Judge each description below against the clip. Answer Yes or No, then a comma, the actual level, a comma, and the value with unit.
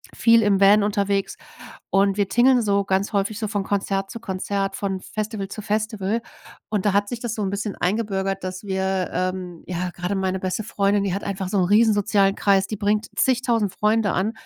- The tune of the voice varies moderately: No, narrow, 1.8 semitones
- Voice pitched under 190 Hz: No, high, 200 Hz